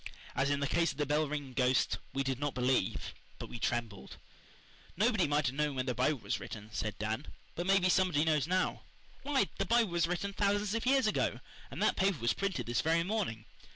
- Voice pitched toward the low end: No, medium, 150 Hz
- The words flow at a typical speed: No, fast, 215 wpm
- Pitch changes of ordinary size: No, wide, 6.9 semitones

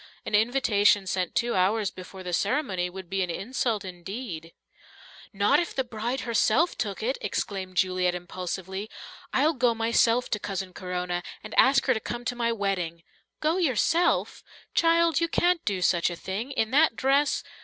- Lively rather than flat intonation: Yes, wide, 5.8 semitones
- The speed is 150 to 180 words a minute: Yes, average, 165 wpm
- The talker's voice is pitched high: Yes, high, 215 Hz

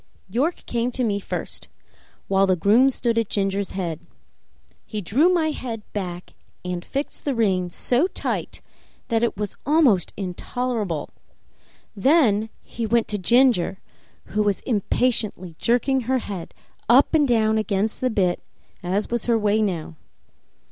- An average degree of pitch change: Yes, average, 4.3 semitones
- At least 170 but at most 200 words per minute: No, average, 145 wpm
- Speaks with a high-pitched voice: Yes, high, 220 Hz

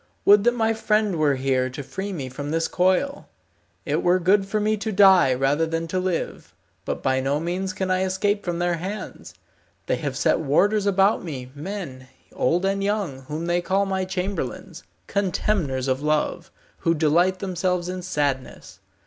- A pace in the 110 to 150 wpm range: No, average, 175 wpm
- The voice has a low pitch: No, medium, 180 Hz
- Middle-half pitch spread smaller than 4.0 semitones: No, average, 4.7 semitones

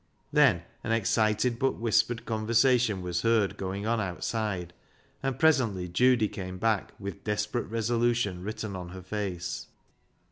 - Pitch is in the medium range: No, low, 110 Hz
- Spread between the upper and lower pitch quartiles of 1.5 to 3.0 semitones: No, average, 3.7 semitones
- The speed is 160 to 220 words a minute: No, slow, 135 wpm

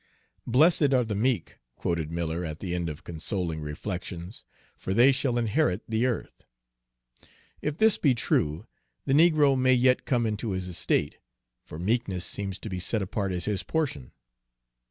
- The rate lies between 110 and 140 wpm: No, average, 165 wpm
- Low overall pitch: Yes, low, 105 Hz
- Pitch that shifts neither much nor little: No, wide, 6.4 semitones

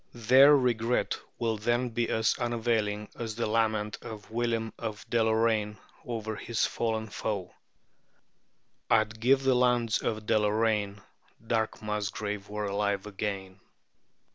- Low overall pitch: Yes, low, 110 Hz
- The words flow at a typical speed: No, slow, 120 wpm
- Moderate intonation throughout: No, narrow, 1.9 semitones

